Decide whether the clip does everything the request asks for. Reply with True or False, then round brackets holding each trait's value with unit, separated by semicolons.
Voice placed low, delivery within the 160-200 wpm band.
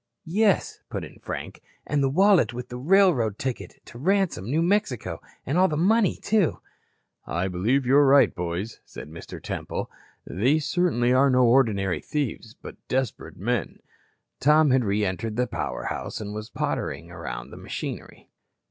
True (130 Hz; 165 wpm)